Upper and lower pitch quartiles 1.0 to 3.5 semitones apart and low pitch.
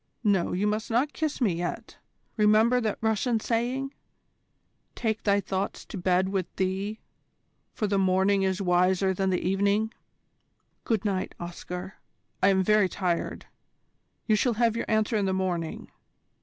No: average, 2.7 semitones; high, 200 Hz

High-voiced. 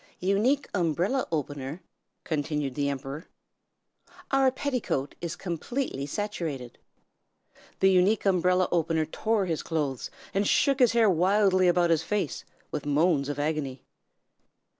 No: medium, 175 Hz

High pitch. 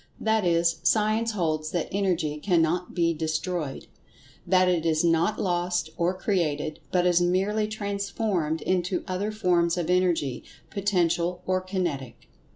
No: medium, 180 Hz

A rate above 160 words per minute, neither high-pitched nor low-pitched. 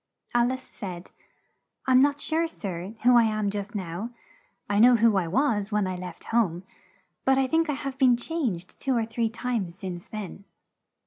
No: average, 185 wpm; high, 225 Hz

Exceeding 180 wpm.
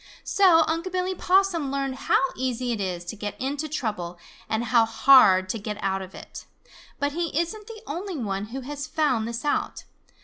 Yes: average, 190 wpm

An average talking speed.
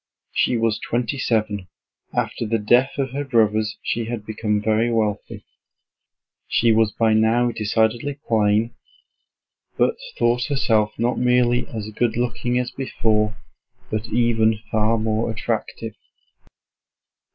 No: slow, 125 wpm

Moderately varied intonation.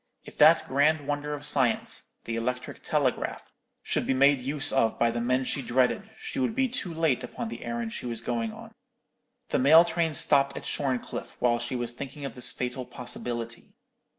Yes: average, 3.5 semitones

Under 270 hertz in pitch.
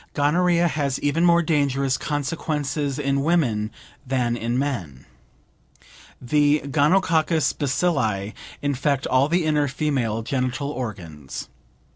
Yes: medium, 140 Hz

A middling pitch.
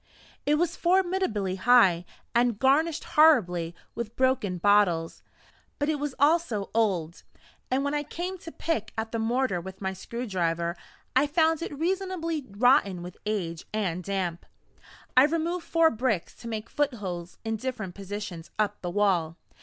No: high, 225 Hz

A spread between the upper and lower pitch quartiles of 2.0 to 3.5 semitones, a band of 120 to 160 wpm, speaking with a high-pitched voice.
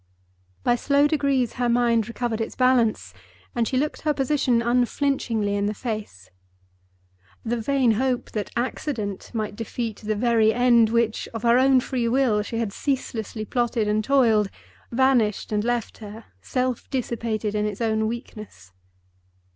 Yes: average, 2.8 semitones; average, 155 wpm; high, 235 Hz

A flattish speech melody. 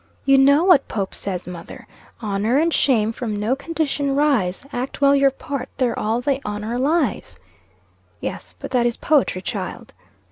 No: average, 4.7 semitones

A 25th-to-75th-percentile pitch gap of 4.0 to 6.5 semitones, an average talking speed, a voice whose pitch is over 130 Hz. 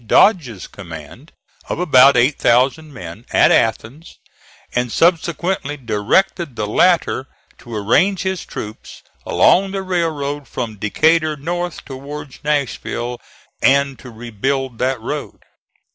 No: wide, 5.6 semitones; slow, 115 wpm; medium, 140 Hz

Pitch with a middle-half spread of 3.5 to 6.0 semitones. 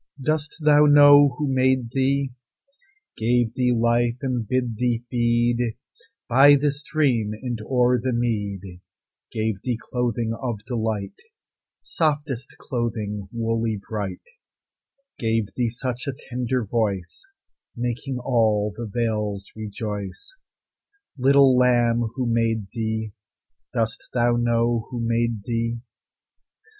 No: narrow, 2.4 semitones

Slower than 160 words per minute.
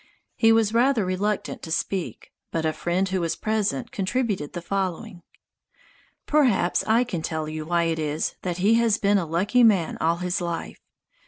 No: average, 175 wpm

